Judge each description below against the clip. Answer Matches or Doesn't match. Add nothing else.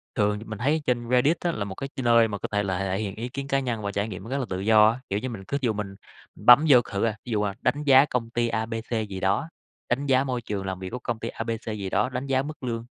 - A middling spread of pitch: Matches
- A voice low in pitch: Matches